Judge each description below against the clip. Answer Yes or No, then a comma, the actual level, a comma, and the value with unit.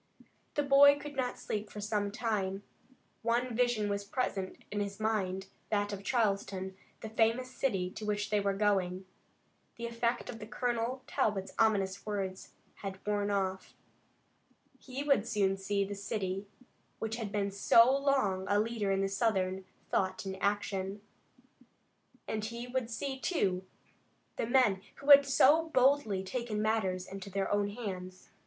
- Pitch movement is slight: No, average, 3.3 semitones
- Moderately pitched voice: No, high, 210 Hz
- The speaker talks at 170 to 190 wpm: No, average, 150 wpm